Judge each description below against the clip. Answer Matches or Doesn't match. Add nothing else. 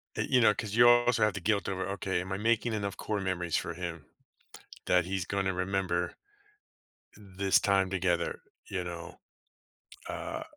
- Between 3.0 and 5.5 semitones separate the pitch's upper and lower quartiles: Doesn't match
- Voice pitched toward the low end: Matches